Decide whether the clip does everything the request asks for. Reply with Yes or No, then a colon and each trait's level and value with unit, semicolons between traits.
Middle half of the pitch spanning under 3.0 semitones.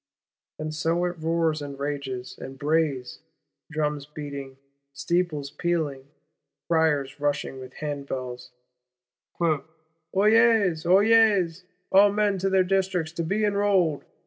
No: average, 4.3 semitones